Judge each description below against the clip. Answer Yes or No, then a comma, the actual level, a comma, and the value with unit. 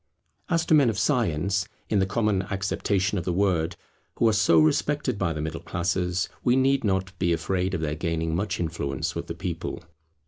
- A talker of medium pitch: No, very low, 95 Hz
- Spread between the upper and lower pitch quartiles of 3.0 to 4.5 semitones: Yes, average, 3.9 semitones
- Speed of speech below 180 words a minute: No, average, 195 wpm